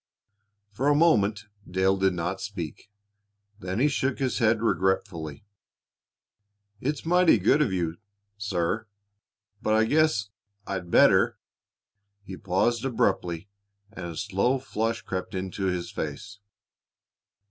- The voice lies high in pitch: No, low, 100 Hz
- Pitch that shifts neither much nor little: Yes, average, 3.9 semitones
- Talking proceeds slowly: Yes, slow, 125 wpm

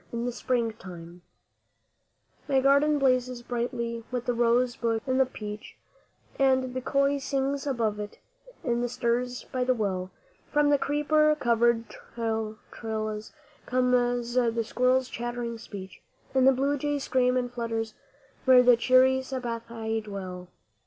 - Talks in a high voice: Yes, high, 245 Hz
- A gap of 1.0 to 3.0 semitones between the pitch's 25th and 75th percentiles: Yes, narrow, 2.4 semitones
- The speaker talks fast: No, average, 140 wpm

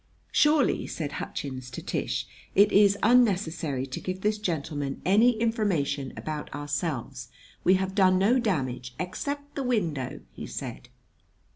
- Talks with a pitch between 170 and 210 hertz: Yes, medium, 185 Hz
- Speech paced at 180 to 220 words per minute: No, average, 140 wpm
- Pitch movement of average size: No, wide, 7.0 semitones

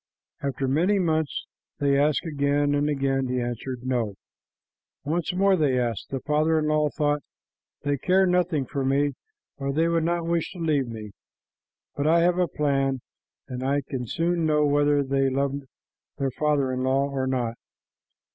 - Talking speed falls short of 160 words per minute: No, average, 170 wpm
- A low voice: No, medium, 145 Hz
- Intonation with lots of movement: No, average, 3.0 semitones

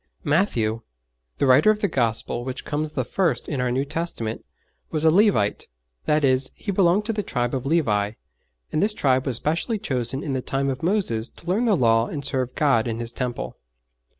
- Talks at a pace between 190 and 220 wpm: Yes, average, 200 wpm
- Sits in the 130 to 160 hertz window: Yes, low, 135 Hz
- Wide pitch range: Yes, wide, 5.7 semitones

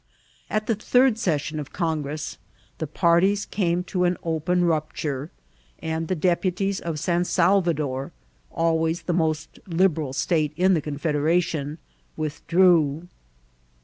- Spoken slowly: Yes, slow, 130 wpm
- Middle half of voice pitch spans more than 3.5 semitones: No, average, 2.8 semitones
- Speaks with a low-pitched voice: No, medium, 165 Hz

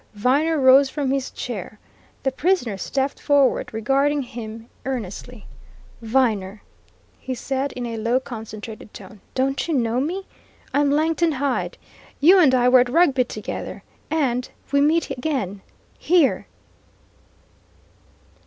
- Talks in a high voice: Yes, very high, 260 Hz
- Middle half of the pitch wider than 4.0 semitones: No, average, 3.7 semitones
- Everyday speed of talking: No, slow, 125 wpm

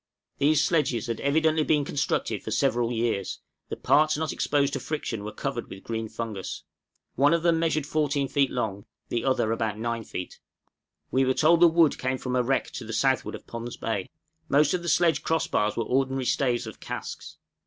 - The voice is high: No, low, 135 Hz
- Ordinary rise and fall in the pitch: Yes, average, 4.8 semitones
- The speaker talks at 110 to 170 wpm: No, average, 195 wpm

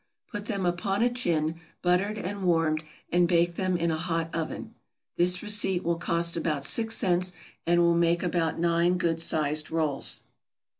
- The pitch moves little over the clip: Yes, narrow, 1.9 semitones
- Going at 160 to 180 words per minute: Yes, average, 165 wpm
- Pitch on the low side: No, medium, 170 Hz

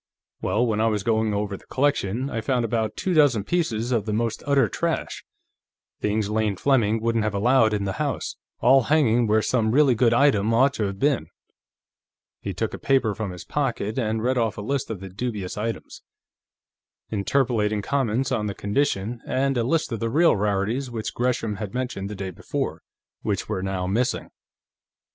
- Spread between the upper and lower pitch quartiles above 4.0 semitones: No, average, 3.6 semitones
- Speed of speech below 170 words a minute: No, average, 185 wpm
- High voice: No, low, 115 Hz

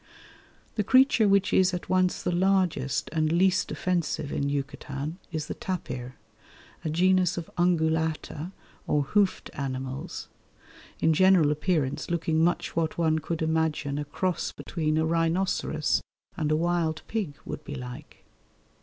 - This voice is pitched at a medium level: Yes, medium, 160 Hz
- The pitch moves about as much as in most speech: Yes, average, 3.3 semitones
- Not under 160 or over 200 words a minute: No, average, 140 wpm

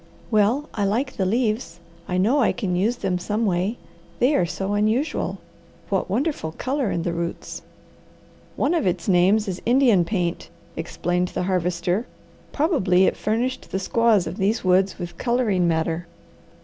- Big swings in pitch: No, average, 4.9 semitones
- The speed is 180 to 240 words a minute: No, average, 160 wpm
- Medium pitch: No, high, 195 Hz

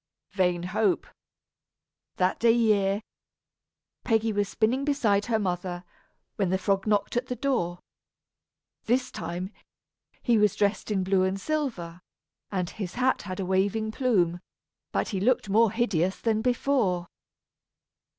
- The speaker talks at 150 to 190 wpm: No, slow, 135 wpm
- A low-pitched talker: No, high, 205 Hz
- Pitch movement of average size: Yes, average, 3.9 semitones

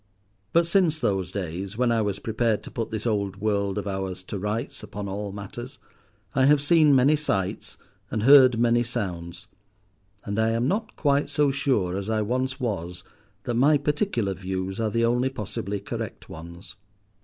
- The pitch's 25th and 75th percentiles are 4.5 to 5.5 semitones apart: Yes, average, 5.0 semitones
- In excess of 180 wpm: No, average, 175 wpm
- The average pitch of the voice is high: No, low, 110 Hz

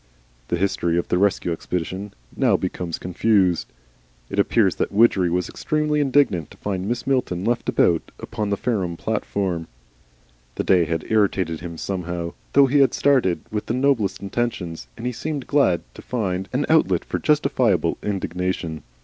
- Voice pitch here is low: Yes, low, 100 Hz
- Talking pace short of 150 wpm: No, average, 160 wpm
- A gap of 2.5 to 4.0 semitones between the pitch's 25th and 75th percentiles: No, wide, 5.5 semitones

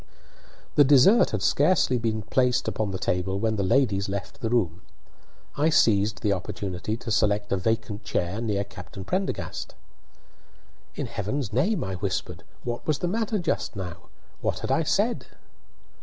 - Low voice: Yes, low, 110 Hz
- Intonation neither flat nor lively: Yes, average, 4.9 semitones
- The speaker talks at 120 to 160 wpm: Yes, average, 155 wpm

